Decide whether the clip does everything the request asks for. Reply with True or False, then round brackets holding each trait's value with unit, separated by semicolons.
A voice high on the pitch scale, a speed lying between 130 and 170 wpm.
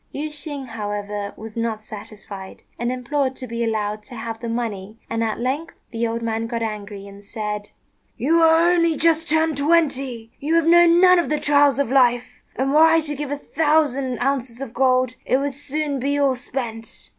False (255 Hz; 195 wpm)